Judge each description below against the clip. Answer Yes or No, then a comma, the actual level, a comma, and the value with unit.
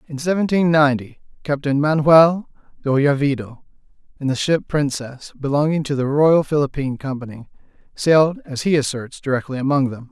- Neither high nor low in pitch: Yes, medium, 145 Hz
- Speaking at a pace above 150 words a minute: No, average, 140 wpm